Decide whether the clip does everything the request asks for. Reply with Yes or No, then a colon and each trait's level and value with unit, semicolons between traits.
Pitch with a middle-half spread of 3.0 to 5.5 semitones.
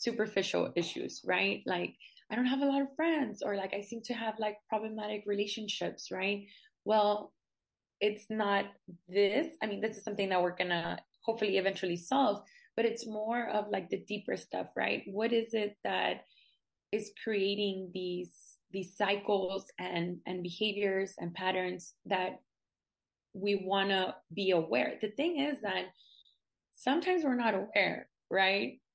No: narrow, 2.6 semitones